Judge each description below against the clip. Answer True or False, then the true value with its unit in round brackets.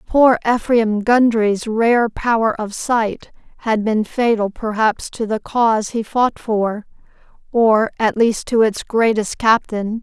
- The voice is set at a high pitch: True (225 Hz)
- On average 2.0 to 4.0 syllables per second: True (3.7 syllables/s)